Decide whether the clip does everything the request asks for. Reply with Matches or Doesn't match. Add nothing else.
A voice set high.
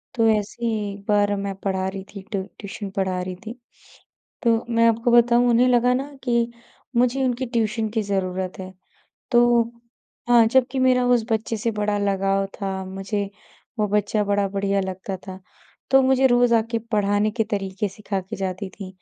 Matches